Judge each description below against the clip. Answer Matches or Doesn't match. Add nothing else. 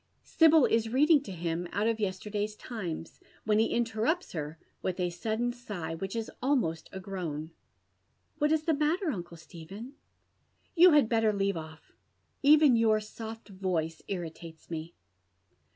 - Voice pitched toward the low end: Doesn't match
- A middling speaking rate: Matches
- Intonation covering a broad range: Matches